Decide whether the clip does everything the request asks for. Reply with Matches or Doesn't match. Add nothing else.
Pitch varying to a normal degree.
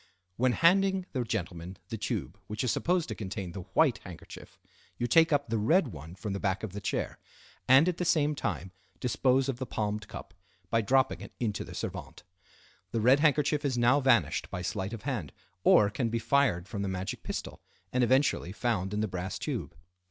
Doesn't match